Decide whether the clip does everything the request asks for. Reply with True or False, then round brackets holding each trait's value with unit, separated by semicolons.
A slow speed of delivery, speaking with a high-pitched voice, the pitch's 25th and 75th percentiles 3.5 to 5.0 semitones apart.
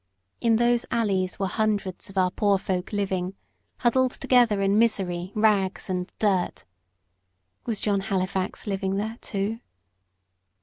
False (130 wpm; 200 Hz; 2.7 semitones)